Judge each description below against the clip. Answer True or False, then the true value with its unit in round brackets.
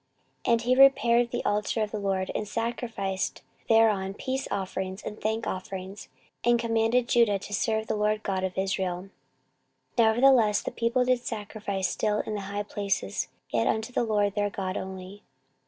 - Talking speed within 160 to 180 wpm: True (170 wpm)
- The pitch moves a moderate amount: True (3.1 semitones)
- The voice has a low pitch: False (210 Hz)